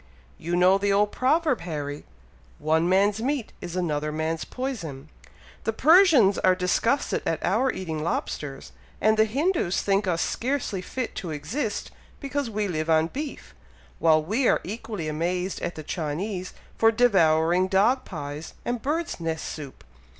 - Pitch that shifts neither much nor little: No, wide, 6.5 semitones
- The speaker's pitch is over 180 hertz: Yes, high, 190 Hz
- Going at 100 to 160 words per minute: Yes, average, 150 wpm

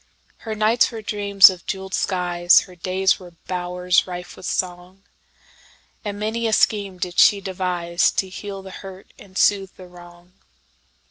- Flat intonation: Yes, narrow, 2.0 semitones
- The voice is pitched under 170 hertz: No, medium, 185 Hz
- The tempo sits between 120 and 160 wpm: Yes, average, 140 wpm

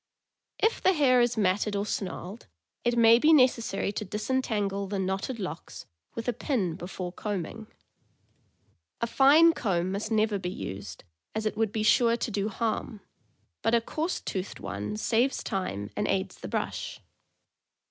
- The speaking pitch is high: Yes, high, 215 Hz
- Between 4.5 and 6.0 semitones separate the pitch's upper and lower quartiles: No, average, 3.7 semitones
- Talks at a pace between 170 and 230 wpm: No, average, 155 wpm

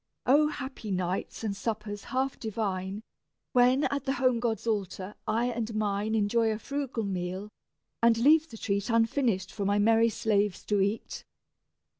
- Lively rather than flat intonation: No, average, 3.3 semitones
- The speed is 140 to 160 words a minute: Yes, average, 155 wpm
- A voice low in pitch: No, high, 220 Hz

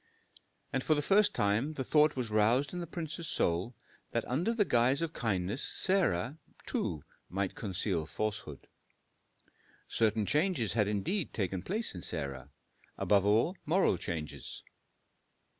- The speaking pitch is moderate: No, low, 115 Hz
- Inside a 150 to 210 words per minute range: No, average, 140 wpm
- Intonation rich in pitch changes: Yes, wide, 8.3 semitones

